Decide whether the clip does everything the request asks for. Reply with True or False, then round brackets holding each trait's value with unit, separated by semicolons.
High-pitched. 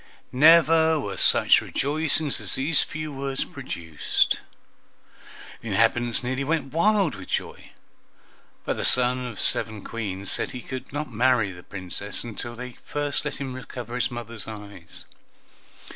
False (125 Hz)